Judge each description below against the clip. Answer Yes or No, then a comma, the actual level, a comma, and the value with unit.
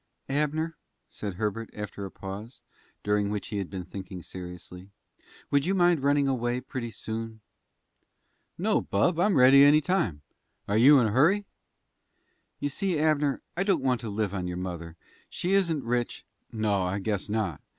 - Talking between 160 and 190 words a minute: Yes, average, 170 wpm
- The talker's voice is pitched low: Yes, low, 115 Hz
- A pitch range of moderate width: No, wide, 6.5 semitones